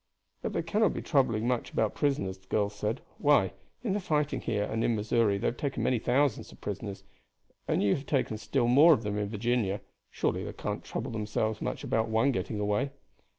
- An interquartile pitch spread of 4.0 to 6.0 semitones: Yes, average, 4.6 semitones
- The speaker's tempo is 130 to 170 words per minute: No, fast, 205 wpm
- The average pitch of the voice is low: Yes, low, 115 Hz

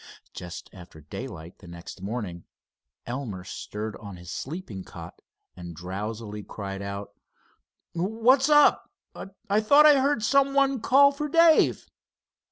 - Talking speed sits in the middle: No, slow, 130 wpm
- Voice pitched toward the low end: Yes, low, 110 Hz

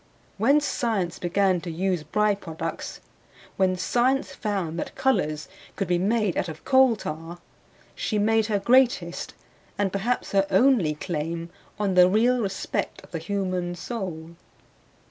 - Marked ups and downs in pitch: No, average, 4.4 semitones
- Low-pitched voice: No, high, 190 Hz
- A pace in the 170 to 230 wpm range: No, average, 140 wpm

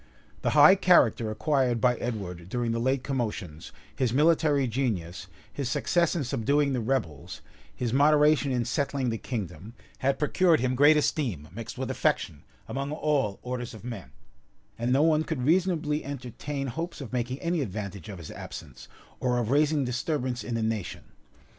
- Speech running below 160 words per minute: No, average, 165 wpm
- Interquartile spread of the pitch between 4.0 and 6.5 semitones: Yes, average, 4.6 semitones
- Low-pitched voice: Yes, low, 125 Hz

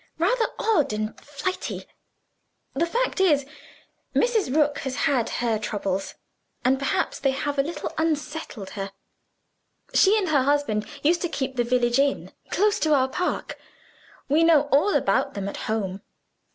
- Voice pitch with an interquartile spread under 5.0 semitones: No, wide, 5.6 semitones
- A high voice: Yes, very high, 280 Hz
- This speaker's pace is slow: No, average, 150 wpm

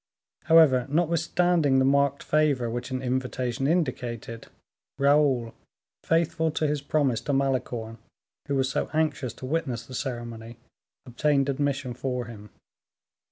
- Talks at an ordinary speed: No, slow, 125 wpm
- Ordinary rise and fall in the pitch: Yes, average, 3.5 semitones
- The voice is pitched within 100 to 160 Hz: Yes, low, 135 Hz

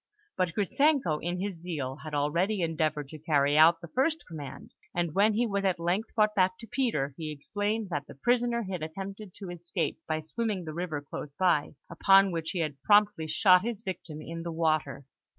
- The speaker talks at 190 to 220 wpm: Yes, average, 195 wpm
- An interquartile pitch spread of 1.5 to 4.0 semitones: No, average, 4.7 semitones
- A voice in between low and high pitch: Yes, medium, 175 Hz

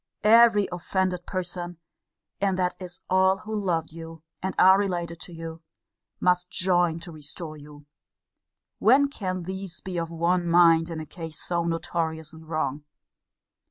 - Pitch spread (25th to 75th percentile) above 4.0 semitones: No, narrow, 2.4 semitones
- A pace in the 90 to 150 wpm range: Yes, average, 145 wpm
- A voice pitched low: No, medium, 175 Hz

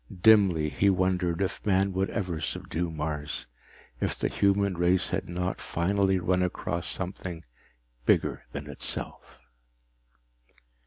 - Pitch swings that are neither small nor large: No, narrow, 2.3 semitones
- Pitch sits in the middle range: No, very low, 90 Hz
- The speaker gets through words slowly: Yes, slow, 120 wpm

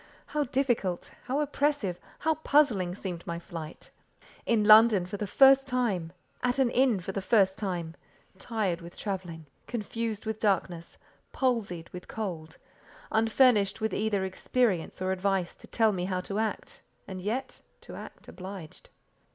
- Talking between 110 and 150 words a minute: Yes, average, 145 wpm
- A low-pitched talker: No, high, 205 Hz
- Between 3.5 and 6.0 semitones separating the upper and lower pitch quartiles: Yes, average, 4.5 semitones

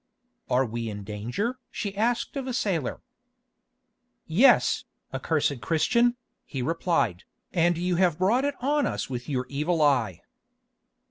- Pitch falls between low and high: Yes, medium, 165 Hz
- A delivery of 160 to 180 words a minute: No, slow, 135 wpm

